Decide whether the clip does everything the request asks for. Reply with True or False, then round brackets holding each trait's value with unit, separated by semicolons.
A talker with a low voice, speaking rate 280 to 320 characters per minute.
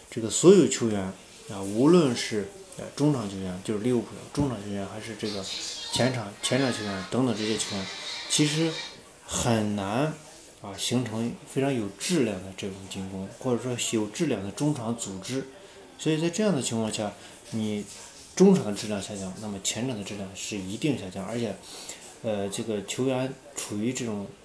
False (110 Hz; 270 characters per minute)